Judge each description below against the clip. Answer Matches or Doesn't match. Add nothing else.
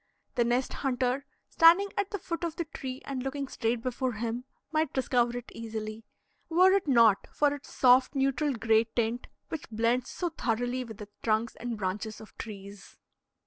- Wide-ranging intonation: Doesn't match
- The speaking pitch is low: Doesn't match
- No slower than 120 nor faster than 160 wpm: Doesn't match